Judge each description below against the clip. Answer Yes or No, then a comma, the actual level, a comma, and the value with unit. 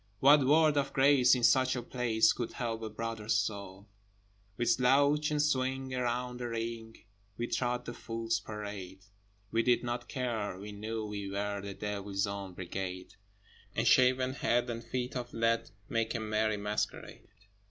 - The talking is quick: No, average, 165 wpm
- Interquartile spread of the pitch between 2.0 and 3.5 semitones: Yes, average, 3.2 semitones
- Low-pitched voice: Yes, low, 115 Hz